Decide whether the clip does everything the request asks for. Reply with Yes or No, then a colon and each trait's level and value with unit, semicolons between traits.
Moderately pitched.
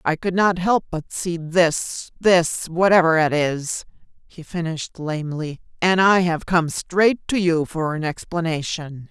Yes: medium, 170 Hz